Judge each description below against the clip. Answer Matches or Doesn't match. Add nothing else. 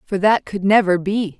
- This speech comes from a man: Doesn't match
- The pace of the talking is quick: Matches